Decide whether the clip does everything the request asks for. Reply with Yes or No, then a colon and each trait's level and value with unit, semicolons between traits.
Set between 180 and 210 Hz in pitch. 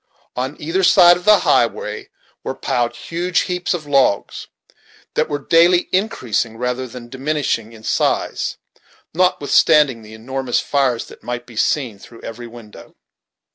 No: low, 130 Hz